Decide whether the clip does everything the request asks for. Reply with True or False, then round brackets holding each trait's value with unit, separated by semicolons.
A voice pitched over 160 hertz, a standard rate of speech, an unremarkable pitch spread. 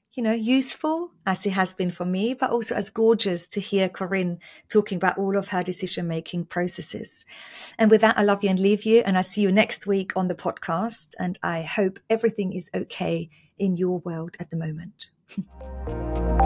True (190 Hz; 195 wpm; 3.1 semitones)